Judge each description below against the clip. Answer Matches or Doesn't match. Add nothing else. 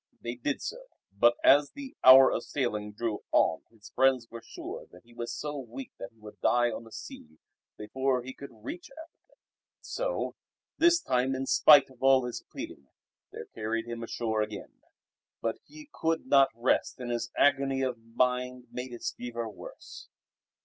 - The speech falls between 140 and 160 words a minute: Doesn't match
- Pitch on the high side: Doesn't match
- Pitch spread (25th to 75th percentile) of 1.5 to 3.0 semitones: Matches